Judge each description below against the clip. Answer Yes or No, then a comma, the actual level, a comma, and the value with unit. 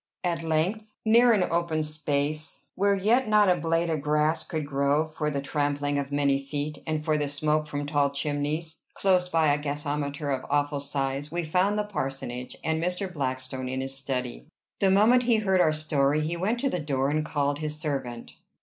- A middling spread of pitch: Yes, average, 3.2 semitones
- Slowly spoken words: No, average, 195 wpm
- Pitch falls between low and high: Yes, medium, 150 Hz